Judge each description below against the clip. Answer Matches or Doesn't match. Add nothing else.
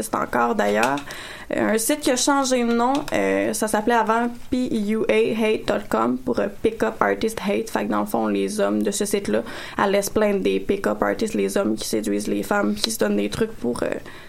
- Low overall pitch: Doesn't match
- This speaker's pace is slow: Doesn't match